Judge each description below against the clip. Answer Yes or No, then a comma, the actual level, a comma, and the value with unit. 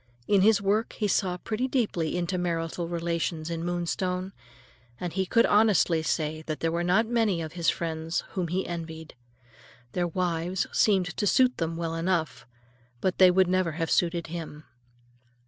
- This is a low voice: No, medium, 175 Hz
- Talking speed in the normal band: Yes, average, 165 wpm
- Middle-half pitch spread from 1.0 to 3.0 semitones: Yes, narrow, 2.4 semitones